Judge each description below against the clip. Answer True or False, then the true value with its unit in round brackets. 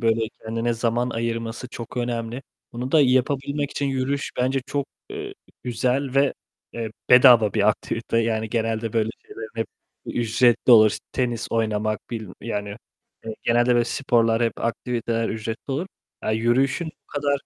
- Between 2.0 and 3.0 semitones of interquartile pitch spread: True (2.4 semitones)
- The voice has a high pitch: False (120 Hz)